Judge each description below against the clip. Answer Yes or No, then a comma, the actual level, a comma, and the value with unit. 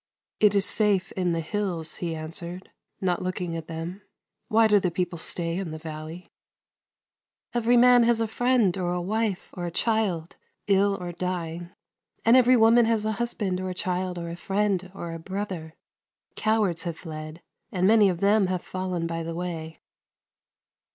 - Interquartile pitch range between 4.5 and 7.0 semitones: No, average, 3.7 semitones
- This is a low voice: No, medium, 185 Hz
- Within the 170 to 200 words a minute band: Yes, average, 185 wpm